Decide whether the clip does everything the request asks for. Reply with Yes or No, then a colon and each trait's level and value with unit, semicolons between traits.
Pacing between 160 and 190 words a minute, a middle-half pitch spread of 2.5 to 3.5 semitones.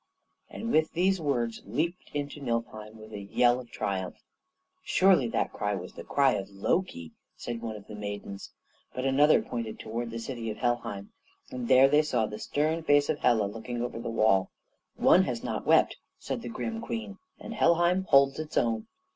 No: average, 185 wpm; average, 4.9 semitones